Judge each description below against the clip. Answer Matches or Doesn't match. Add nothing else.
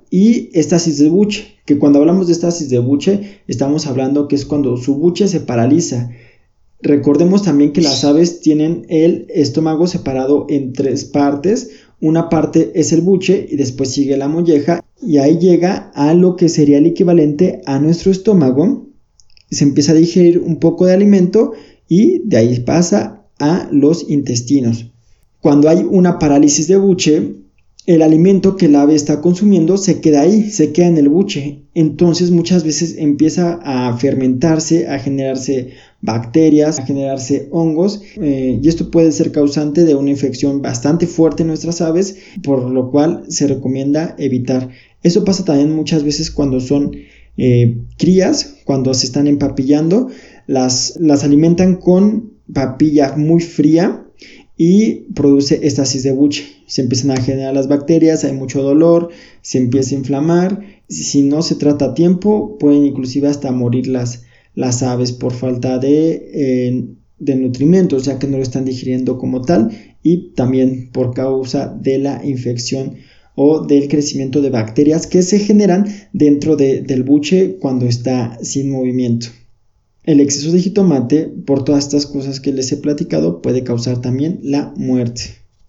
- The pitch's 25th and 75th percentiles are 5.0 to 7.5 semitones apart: Doesn't match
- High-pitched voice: Doesn't match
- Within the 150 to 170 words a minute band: Matches